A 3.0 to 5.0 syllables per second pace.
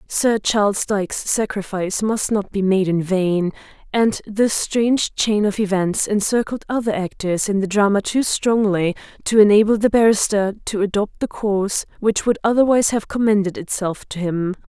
Yes: 4.9 syllables/s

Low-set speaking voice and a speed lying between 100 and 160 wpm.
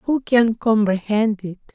No: high, 220 Hz; average, 140 wpm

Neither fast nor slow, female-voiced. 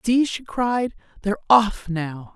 Yes: average, 155 wpm; female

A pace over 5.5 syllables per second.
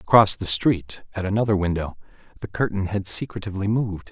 Yes: 6.0 syllables/s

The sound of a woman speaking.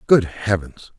No: male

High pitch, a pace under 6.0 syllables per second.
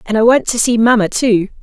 Yes: high, 225 Hz; 5.7 syllables/s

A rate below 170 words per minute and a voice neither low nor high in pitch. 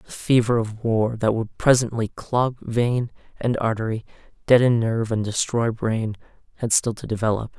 No: average, 160 wpm; low, 115 Hz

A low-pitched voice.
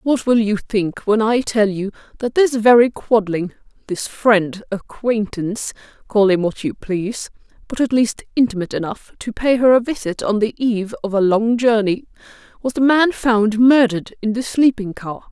No: high, 220 Hz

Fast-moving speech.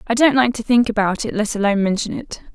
Yes: fast, 260 wpm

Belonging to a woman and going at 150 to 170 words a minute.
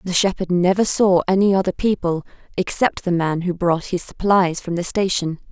No: female; average, 185 wpm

